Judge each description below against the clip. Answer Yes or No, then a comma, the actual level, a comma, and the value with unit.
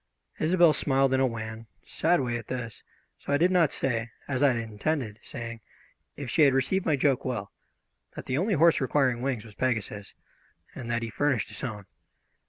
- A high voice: No, low, 130 Hz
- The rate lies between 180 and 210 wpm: Yes, average, 190 wpm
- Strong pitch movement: No, average, 3.9 semitones